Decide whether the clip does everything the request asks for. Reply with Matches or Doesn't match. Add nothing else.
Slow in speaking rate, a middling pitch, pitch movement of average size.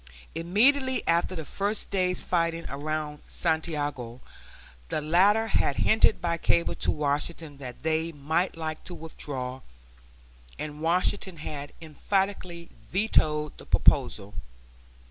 Matches